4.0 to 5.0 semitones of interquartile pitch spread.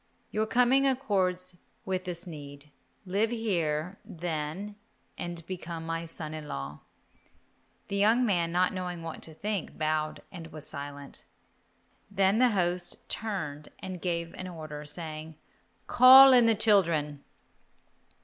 Yes: average, 4.5 semitones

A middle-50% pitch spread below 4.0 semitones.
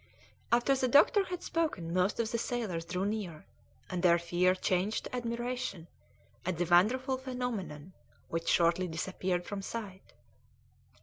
No: wide, 5.5 semitones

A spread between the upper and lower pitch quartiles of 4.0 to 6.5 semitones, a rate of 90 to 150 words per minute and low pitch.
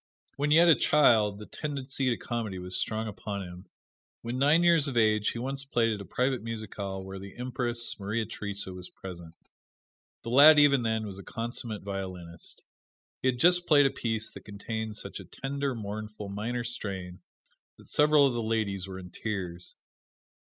No: average, 4.7 semitones; average, 180 wpm; low, 110 Hz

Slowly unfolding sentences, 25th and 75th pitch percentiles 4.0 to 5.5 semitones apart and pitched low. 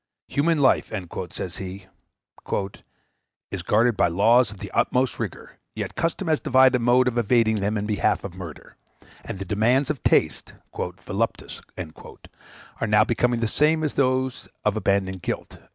No: average, 155 wpm; average, 4.3 semitones; low, 115 Hz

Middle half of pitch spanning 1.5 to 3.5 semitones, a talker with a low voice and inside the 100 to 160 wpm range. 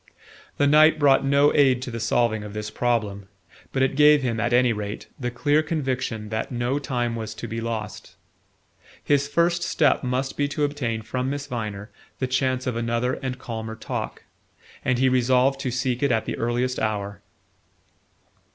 No: average, 3.2 semitones; low, 125 Hz; average, 180 wpm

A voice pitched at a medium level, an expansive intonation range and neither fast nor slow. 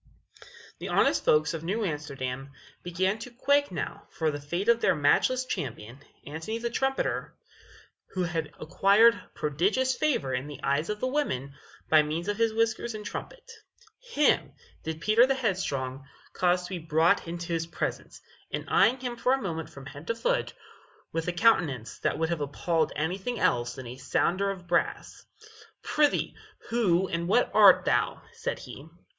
Yes: medium, 175 Hz; wide, 7.2 semitones; average, 170 wpm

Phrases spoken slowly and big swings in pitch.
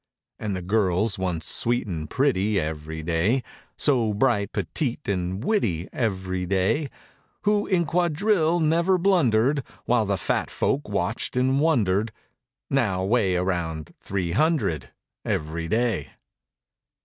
Yes: slow, 125 wpm; wide, 7.4 semitones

